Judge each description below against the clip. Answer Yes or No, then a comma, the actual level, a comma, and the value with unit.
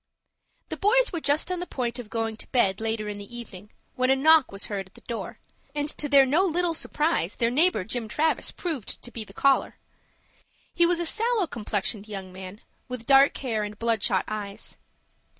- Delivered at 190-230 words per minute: Yes, average, 200 wpm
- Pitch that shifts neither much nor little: No, wide, 6.7 semitones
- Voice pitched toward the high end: Yes, high, 240 Hz